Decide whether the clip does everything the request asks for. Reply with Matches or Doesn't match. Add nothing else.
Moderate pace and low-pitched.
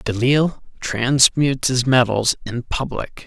Doesn't match